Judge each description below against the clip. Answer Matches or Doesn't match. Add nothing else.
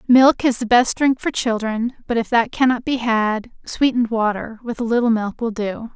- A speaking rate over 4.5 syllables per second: Matches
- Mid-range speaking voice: Doesn't match